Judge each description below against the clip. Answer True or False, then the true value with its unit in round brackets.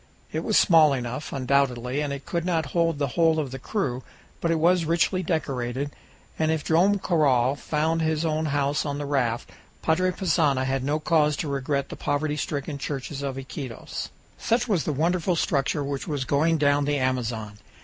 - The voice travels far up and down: False (3.1 semitones)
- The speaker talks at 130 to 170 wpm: False (185 wpm)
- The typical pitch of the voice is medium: True (145 Hz)